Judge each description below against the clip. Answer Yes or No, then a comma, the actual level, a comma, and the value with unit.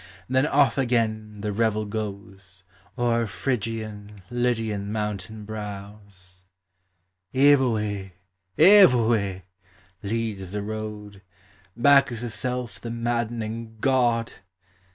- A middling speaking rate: No, slow, 90 wpm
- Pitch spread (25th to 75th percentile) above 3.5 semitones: No, narrow, 2.6 semitones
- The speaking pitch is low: Yes, low, 110 Hz